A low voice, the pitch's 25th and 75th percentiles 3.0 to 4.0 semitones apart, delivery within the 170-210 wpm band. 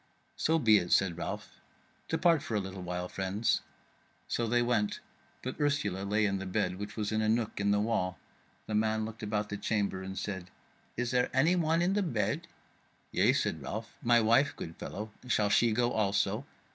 Yes: low, 110 Hz; average, 3.5 semitones; average, 195 wpm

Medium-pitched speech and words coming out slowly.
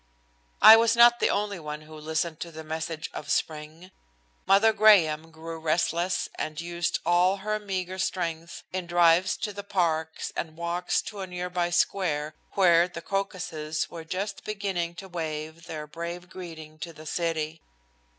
No: medium, 170 Hz; average, 160 wpm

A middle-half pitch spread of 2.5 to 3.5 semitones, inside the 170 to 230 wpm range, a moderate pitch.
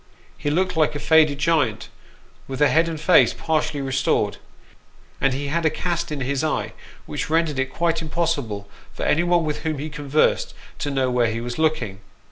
Yes: average, 3.2 semitones; average, 185 wpm; medium, 150 Hz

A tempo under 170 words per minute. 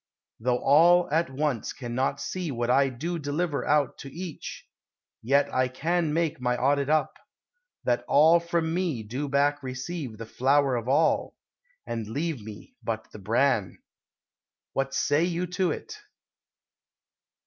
Yes: average, 145 wpm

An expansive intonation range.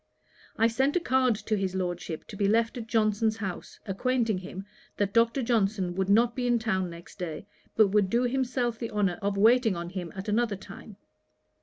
No: average, 3.6 semitones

